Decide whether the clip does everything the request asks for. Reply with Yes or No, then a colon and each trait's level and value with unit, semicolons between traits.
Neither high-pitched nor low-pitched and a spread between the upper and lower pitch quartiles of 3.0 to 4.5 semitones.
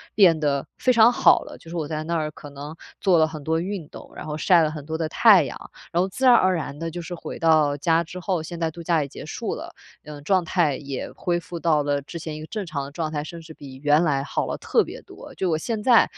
No: medium, 160 Hz; narrow, 2.6 semitones